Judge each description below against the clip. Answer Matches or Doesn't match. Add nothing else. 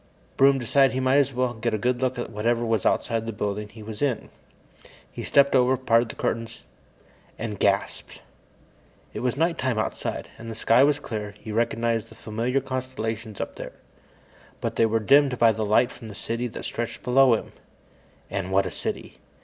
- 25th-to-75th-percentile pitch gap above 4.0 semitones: Doesn't match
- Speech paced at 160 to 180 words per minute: Doesn't match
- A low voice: Matches